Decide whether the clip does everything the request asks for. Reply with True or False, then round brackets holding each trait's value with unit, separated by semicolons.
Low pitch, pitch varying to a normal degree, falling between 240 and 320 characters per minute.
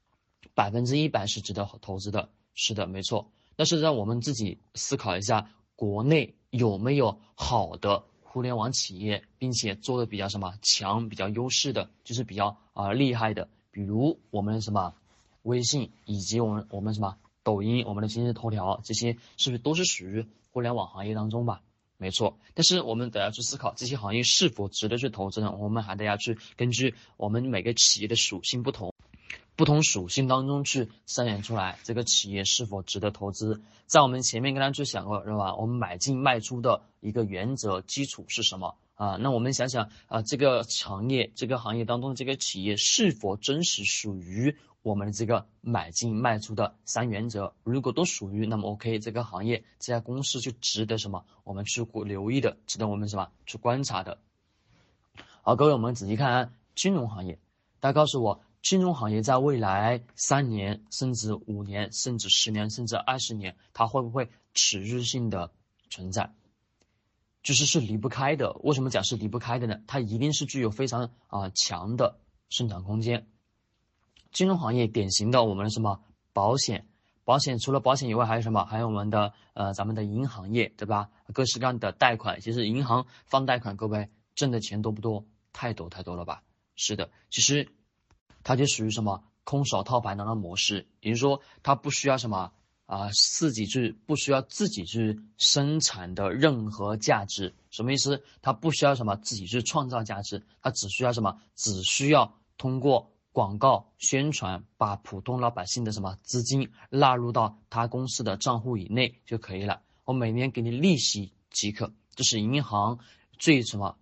True (115 Hz; 3.6 semitones; 285 characters per minute)